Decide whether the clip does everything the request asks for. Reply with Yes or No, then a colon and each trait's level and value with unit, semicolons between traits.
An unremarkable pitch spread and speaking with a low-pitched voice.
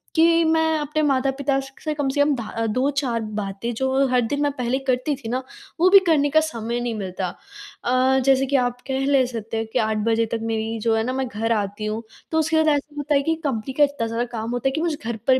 No: average, 4.1 semitones; very high, 260 Hz